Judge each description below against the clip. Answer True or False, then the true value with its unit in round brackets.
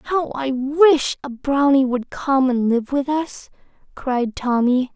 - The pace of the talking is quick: False (160 wpm)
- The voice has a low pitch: False (270 Hz)